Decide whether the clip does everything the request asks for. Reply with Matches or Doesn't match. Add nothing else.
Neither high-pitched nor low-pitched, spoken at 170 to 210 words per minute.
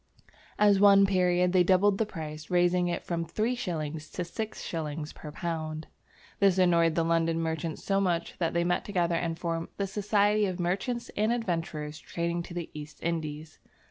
Matches